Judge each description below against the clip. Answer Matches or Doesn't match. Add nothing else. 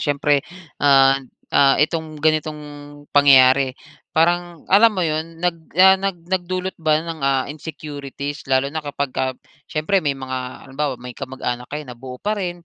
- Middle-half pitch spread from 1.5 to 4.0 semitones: Matches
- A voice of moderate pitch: Matches